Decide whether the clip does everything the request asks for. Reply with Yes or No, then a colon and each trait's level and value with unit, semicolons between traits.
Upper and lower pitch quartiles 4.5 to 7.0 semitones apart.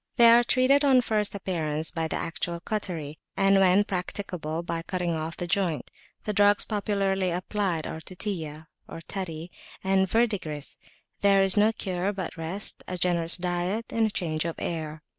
No: average, 3.7 semitones